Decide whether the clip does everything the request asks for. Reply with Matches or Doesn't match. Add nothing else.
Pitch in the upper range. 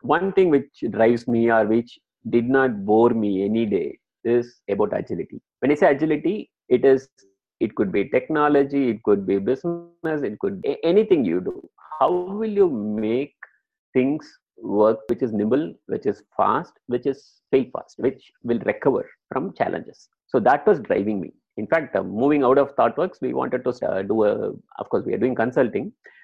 Doesn't match